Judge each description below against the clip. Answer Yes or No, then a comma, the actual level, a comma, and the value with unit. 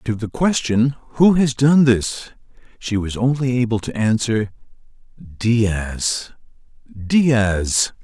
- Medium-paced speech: No, slow, 105 wpm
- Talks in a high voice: No, low, 120 Hz